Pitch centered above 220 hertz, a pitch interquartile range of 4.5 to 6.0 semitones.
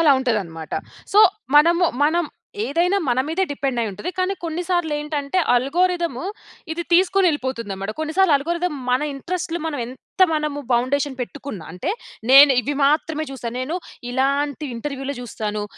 Yes: very high, 290 Hz; average, 4.9 semitones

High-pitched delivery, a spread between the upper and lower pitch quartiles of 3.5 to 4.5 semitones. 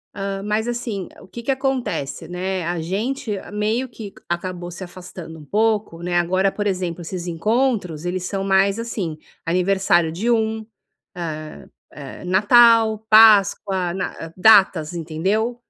Yes: high, 195 Hz; average, 3.9 semitones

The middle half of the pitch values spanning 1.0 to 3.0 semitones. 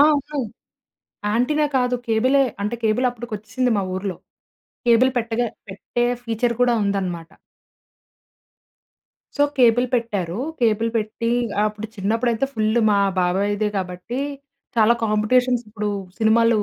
Yes: narrow, 2.6 semitones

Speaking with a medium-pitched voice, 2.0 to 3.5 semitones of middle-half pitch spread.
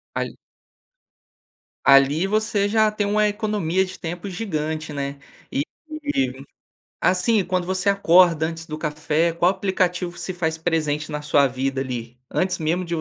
No: medium, 170 Hz; average, 4.0 semitones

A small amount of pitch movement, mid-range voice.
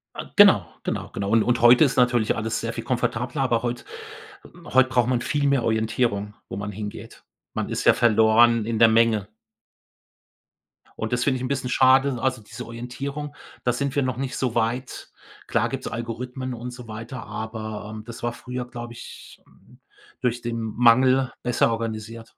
No: narrow, 2.2 semitones; low, 120 Hz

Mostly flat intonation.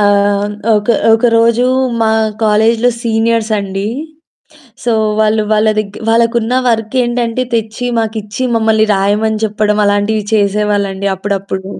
Yes: narrow, 1.9 semitones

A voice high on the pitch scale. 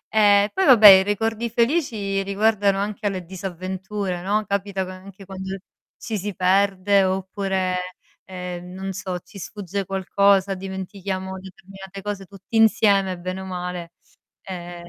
Yes: high, 195 Hz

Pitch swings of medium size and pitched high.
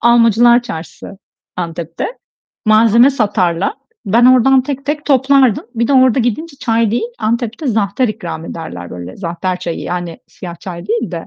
No: wide, 5.8 semitones; high, 225 Hz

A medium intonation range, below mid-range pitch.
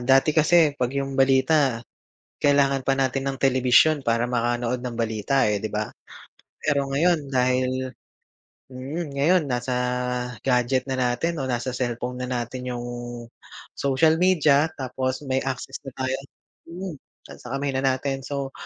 No: narrow, 2.0 semitones; low, 130 Hz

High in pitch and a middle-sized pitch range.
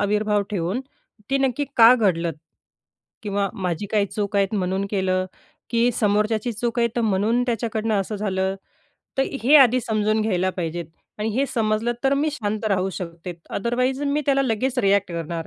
Yes: high, 210 Hz; average, 3.6 semitones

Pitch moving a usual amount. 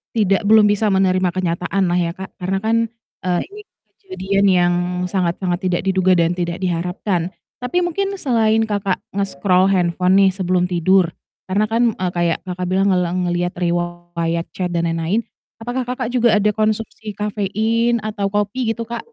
Yes: average, 3.6 semitones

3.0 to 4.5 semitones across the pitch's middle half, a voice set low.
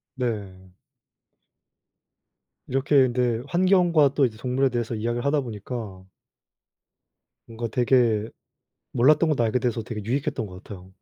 Yes: average, 3.6 semitones; low, 120 Hz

